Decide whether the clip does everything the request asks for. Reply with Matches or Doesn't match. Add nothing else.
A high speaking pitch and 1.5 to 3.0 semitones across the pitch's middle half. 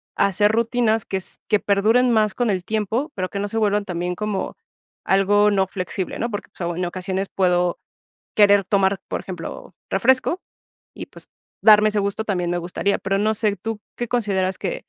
Matches